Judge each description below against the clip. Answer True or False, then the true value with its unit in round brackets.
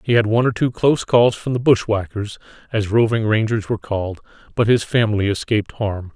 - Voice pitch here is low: True (110 Hz)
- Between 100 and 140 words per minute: False (195 wpm)